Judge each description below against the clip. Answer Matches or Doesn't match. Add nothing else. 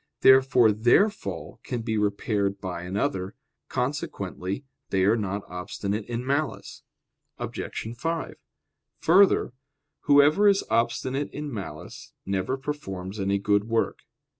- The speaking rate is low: Matches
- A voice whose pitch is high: Doesn't match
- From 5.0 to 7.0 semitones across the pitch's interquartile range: Matches